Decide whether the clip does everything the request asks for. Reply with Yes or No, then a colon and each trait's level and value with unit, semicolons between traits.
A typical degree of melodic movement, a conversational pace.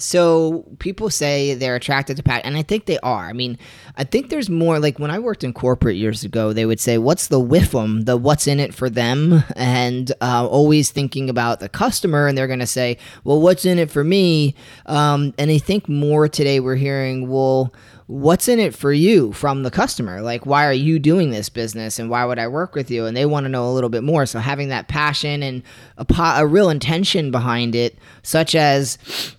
No: average, 3.8 semitones; fast, 225 wpm